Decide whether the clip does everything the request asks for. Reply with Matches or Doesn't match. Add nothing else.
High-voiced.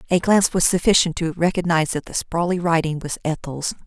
Doesn't match